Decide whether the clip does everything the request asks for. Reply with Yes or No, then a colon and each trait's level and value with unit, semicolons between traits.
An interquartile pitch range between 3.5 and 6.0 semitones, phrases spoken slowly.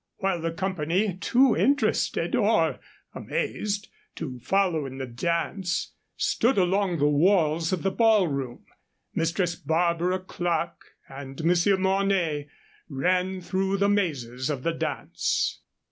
Yes: average, 4.0 semitones; slow, 120 wpm